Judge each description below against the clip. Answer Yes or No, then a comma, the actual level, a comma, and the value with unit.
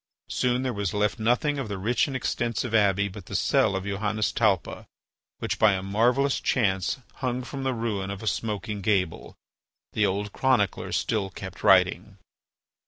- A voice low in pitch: Yes, low, 105 Hz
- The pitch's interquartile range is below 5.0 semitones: Yes, average, 3.6 semitones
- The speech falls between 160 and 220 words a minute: Yes, average, 170 wpm